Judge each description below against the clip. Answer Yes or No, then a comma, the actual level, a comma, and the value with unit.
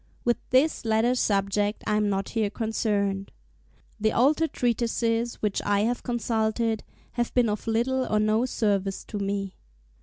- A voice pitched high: Yes, high, 220 Hz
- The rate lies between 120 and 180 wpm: Yes, average, 150 wpm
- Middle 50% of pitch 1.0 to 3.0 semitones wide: Yes, average, 2.7 semitones